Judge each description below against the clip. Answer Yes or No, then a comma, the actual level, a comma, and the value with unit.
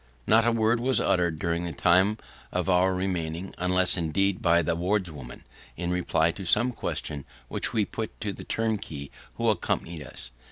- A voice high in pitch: No, very low, 90 Hz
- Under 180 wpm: Yes, average, 170 wpm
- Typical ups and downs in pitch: Yes, average, 3.7 semitones